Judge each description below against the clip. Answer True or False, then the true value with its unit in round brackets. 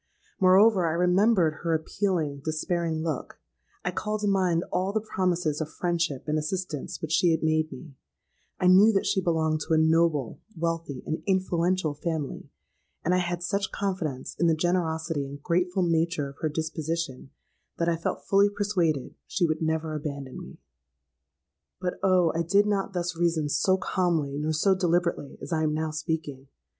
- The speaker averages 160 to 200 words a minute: True (170 wpm)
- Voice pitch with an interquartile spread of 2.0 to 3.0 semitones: True (2.7 semitones)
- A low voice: False (165 Hz)